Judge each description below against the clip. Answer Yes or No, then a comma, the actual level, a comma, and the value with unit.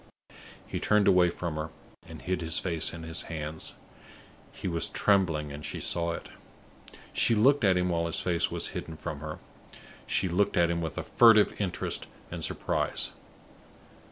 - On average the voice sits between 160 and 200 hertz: No, very low, 85 Hz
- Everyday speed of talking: Yes, average, 170 wpm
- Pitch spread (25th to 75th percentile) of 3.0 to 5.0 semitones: No, narrow, 2.5 semitones